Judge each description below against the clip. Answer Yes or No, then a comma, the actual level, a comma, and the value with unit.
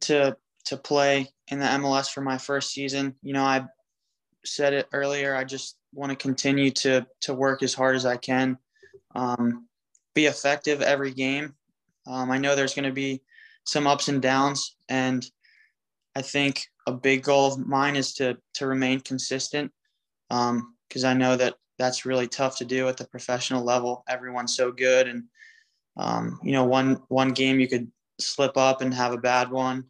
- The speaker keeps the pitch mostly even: Yes, narrow, 1.4 semitones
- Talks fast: No, average, 185 wpm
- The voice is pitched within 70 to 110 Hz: No, low, 135 Hz